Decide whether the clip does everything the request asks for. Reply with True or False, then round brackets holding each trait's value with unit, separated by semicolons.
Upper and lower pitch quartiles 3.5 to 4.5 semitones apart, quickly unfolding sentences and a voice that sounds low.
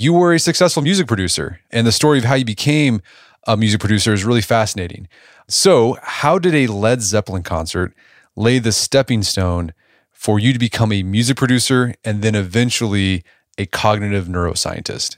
False (4.1 semitones; 170 wpm; 110 Hz)